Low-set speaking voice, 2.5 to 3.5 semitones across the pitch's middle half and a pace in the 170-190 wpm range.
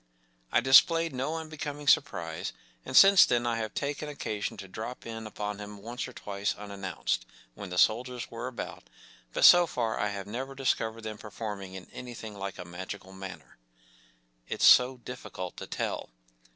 No: low, 110 Hz; average, 4.1 semitones; average, 175 wpm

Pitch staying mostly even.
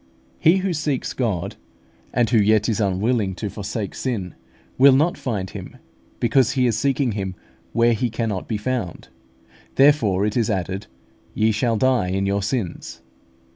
No: average, 4.4 semitones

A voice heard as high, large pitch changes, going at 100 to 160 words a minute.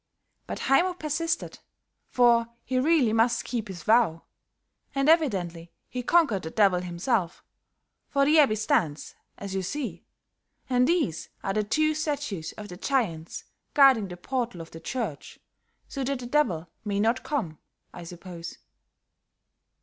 Yes: high, 230 Hz; wide, 7.7 semitones; average, 145 wpm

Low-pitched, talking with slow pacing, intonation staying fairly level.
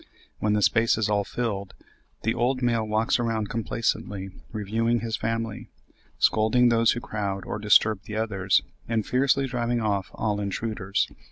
No: low, 110 Hz; average, 155 wpm; narrow, 2.1 semitones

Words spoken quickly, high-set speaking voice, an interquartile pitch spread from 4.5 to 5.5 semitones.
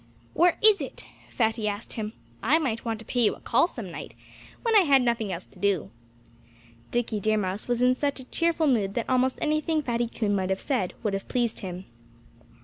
Yes: fast, 210 wpm; high, 235 Hz; average, 4.9 semitones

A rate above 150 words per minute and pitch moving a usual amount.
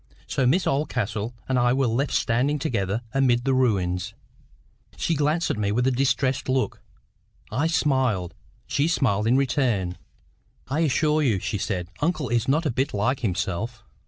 Yes: average, 160 wpm; average, 4.5 semitones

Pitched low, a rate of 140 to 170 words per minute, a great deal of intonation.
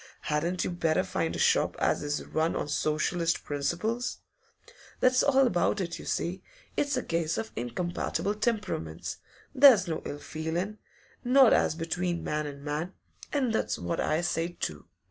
No: medium, 170 Hz; average, 160 wpm; wide, 5.8 semitones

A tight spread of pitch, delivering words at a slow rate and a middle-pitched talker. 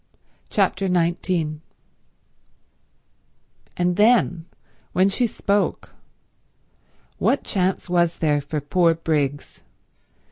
No: average, 3.3 semitones; slow, 80 wpm; medium, 175 Hz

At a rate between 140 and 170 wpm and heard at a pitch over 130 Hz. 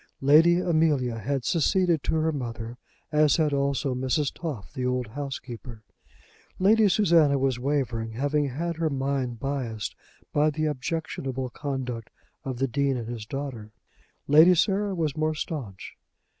Yes: average, 145 wpm; medium, 140 Hz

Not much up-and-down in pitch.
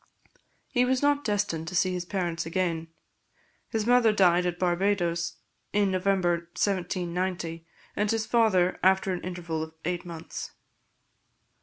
No: average, 3.0 semitones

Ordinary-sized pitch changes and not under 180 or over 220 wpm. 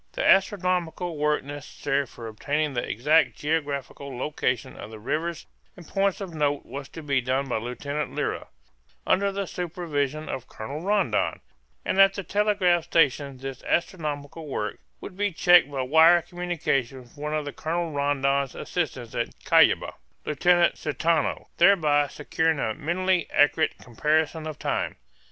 No: average, 3.8 semitones; average, 145 wpm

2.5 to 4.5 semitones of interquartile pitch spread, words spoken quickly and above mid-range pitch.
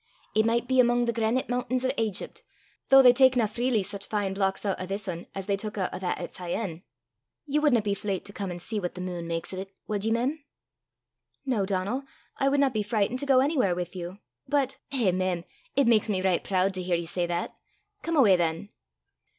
No: average, 5.1 semitones; fast, 230 wpm; high, 205 Hz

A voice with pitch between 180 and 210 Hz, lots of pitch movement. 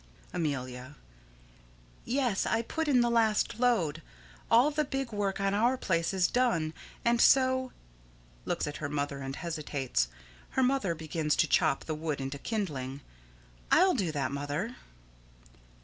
Yes: medium, 185 Hz; wide, 8.7 semitones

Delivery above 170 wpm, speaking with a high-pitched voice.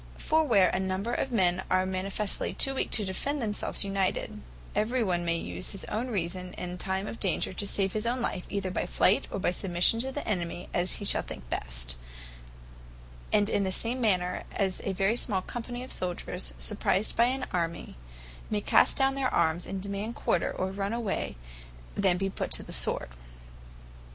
Yes: average, 190 wpm; high, 195 Hz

